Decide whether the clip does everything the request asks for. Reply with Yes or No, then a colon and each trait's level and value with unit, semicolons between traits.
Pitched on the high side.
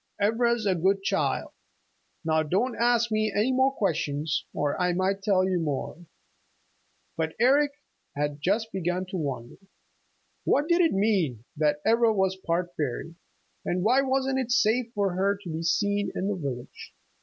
Yes: high, 195 Hz